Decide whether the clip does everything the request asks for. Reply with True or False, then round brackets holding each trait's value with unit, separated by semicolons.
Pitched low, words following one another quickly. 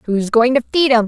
False (240 Hz; 280 wpm)